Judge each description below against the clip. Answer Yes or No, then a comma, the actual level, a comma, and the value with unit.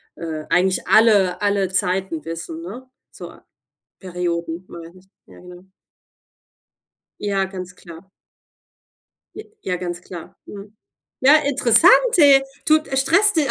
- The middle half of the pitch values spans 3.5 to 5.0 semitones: Yes, average, 4.5 semitones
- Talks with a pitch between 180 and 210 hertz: Yes, high, 190 Hz